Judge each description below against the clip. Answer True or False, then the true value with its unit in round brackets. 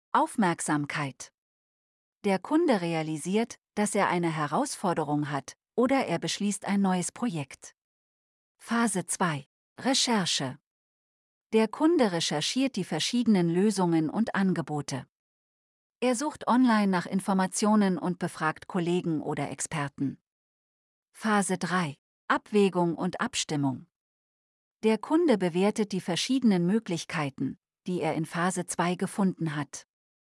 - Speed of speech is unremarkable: False (105 wpm)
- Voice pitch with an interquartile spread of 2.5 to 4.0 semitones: False (5.4 semitones)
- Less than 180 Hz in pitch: False (185 Hz)